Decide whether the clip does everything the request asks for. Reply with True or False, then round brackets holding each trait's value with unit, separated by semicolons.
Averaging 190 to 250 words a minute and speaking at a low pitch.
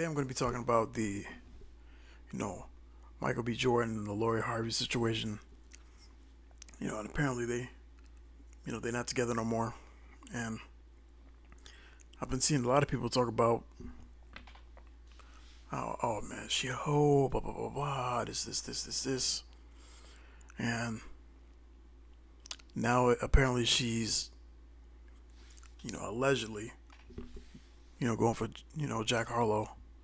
False (140 wpm; 80 Hz)